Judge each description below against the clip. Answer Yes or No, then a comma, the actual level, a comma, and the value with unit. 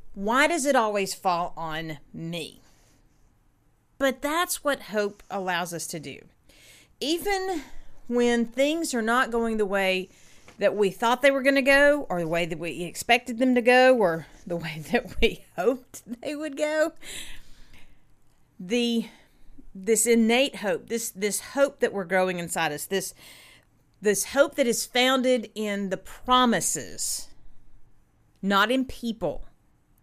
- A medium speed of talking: Yes, average, 145 wpm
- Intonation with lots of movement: Yes, wide, 5.7 semitones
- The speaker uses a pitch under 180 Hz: No, high, 230 Hz